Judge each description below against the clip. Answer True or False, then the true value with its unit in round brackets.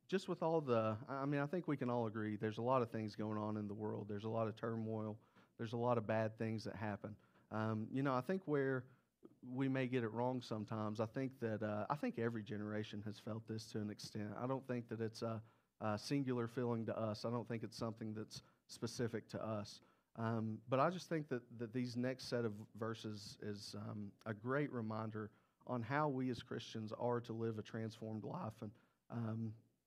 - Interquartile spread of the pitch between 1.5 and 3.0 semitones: True (2.6 semitones)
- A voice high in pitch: False (115 Hz)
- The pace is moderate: False (225 wpm)